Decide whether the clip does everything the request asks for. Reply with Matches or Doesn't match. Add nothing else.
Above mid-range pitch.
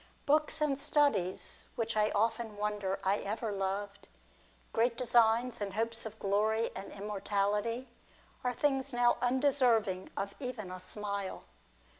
Matches